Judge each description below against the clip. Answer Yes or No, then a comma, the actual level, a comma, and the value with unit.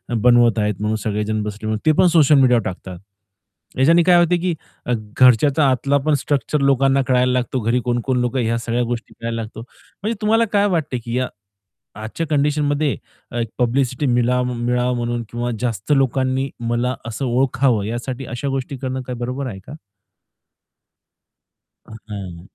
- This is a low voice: Yes, low, 125 Hz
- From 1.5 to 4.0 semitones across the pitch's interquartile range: Yes, average, 2.9 semitones